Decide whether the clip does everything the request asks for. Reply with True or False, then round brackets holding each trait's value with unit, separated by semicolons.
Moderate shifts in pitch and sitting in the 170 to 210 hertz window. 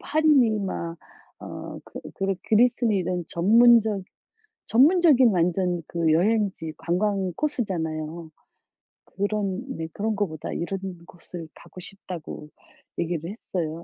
True (4.5 semitones; 190 Hz)